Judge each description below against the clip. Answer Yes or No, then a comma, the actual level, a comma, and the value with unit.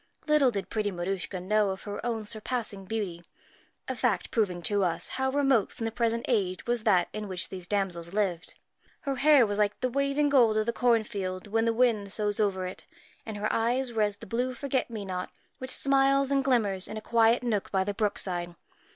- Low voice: No, high, 215 Hz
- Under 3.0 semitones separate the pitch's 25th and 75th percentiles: No, average, 3.9 semitones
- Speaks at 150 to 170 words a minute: No, fast, 205 wpm